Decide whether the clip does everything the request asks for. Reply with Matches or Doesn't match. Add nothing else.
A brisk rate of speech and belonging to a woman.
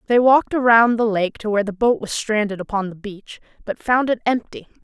Matches